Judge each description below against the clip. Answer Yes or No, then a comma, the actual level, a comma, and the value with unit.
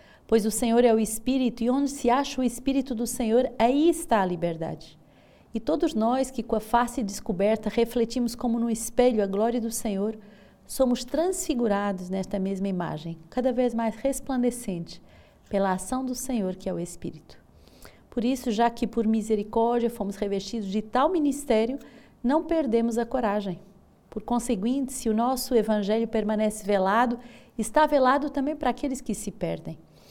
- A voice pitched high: Yes, high, 230 Hz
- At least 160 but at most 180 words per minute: Yes, average, 165 wpm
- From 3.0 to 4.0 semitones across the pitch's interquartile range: Yes, average, 3.5 semitones